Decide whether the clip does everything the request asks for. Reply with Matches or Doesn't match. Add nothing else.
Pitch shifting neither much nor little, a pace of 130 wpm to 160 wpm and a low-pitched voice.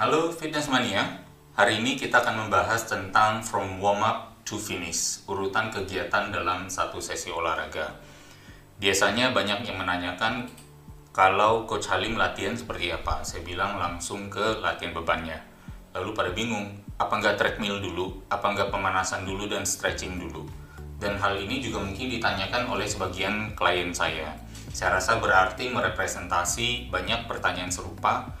Matches